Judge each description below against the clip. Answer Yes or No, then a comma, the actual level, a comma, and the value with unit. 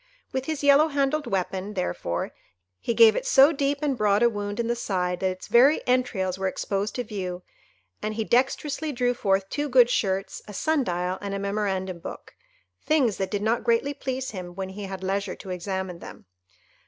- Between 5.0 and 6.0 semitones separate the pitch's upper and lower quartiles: Yes, wide, 5.5 semitones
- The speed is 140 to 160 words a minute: No, average, 195 wpm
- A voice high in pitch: Yes, high, 210 Hz